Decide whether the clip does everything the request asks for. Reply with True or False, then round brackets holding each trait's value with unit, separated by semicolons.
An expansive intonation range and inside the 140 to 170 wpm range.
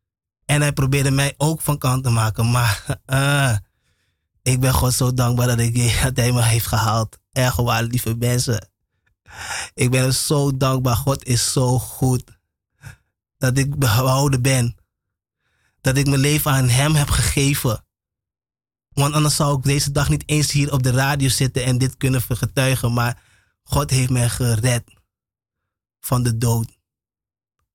False (3.3 semitones; 155 wpm)